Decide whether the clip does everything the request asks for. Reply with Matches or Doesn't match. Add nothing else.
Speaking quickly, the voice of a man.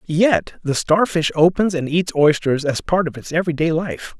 Doesn't match